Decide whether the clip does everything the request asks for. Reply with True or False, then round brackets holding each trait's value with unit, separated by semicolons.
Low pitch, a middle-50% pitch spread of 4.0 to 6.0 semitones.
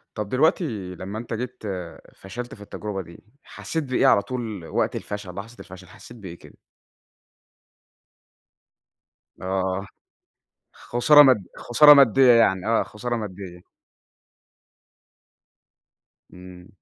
True (105 Hz; 4.6 semitones)